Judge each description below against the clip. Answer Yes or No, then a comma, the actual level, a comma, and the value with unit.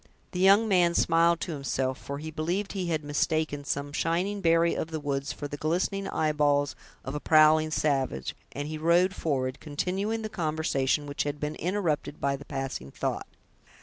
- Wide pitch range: No, average, 3.0 semitones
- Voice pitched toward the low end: No, medium, 155 Hz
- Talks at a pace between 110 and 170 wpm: No, average, 180 wpm